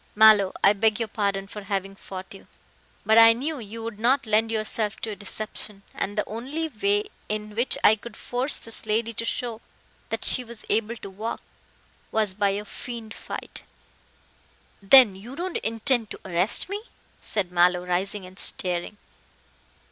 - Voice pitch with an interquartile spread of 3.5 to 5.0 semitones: No, narrow, 2.5 semitones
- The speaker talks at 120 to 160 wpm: No, average, 170 wpm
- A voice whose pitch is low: No, high, 215 Hz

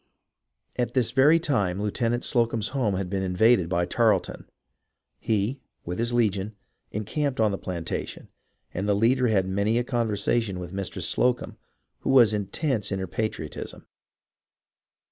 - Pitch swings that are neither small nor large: Yes, average, 3.9 semitones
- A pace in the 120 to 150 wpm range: Yes, average, 145 wpm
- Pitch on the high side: No, low, 110 Hz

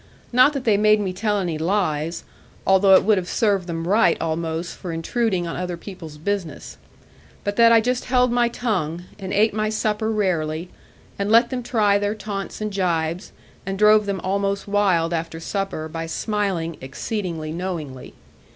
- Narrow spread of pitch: No, average, 4.1 semitones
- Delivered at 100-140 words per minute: No, average, 170 wpm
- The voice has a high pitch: Yes, high, 195 Hz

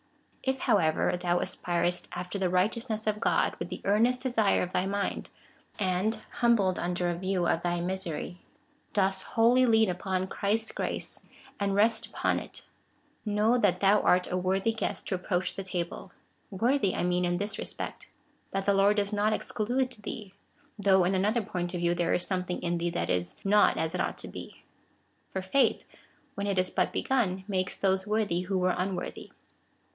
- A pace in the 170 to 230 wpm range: Yes, average, 180 wpm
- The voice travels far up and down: No, average, 2.9 semitones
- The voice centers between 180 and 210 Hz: Yes, high, 190 Hz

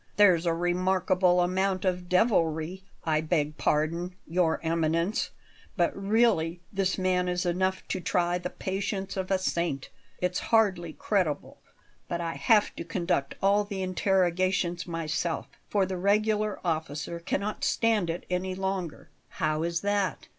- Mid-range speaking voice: Yes, medium, 180 Hz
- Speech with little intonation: Yes, narrow, 2.2 semitones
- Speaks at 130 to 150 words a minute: Yes, average, 140 wpm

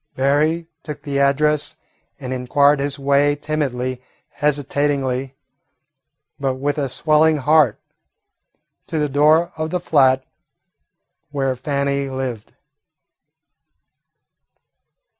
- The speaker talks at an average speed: No, slow, 95 wpm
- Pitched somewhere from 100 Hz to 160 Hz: Yes, medium, 140 Hz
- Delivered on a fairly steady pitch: Yes, narrow, 2.1 semitones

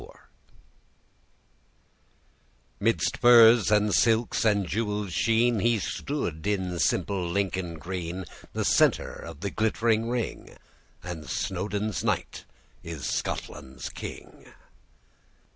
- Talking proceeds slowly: Yes, slow, 95 wpm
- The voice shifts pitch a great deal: No, average, 4.2 semitones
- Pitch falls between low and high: No, low, 100 Hz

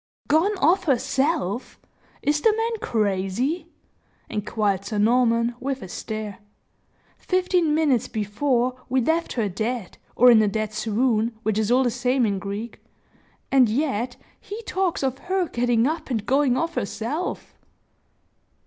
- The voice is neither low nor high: No, high, 245 Hz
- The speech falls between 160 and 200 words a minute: No, average, 140 wpm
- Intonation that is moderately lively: No, wide, 5.8 semitones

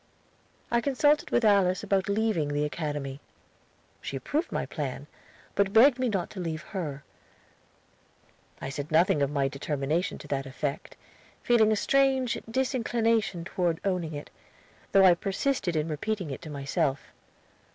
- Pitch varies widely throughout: Yes, wide, 7.0 semitones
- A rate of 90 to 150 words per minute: Yes, average, 145 wpm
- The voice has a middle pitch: Yes, medium, 180 Hz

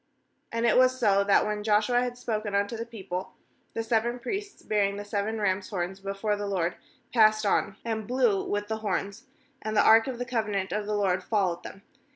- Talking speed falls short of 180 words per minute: No, average, 200 wpm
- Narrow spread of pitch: Yes, narrow, 2.3 semitones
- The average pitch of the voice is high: Yes, high, 210 Hz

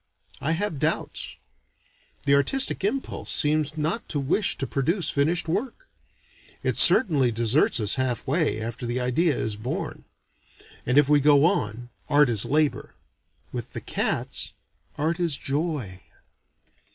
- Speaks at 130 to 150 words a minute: Yes, average, 140 wpm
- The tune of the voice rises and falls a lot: No, average, 4.8 semitones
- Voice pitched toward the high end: No, medium, 145 Hz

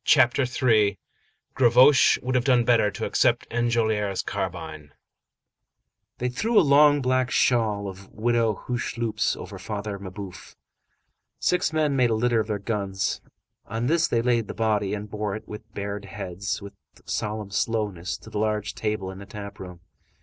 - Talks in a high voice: No, low, 110 Hz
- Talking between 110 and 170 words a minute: Yes, average, 155 wpm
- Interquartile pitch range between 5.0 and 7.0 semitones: No, average, 3.2 semitones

